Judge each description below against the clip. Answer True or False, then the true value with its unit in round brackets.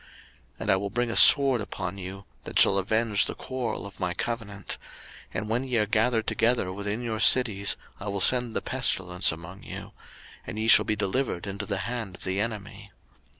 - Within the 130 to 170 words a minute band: False (195 wpm)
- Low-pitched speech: True (105 Hz)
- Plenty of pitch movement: False (3.1 semitones)